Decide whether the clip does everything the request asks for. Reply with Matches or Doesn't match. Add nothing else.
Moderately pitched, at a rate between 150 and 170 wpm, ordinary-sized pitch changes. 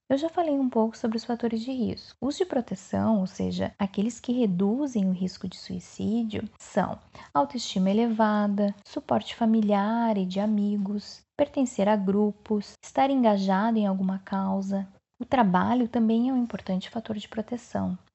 Doesn't match